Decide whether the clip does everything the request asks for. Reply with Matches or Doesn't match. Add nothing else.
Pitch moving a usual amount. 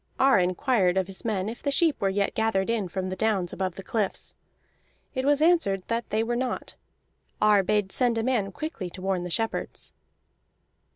Matches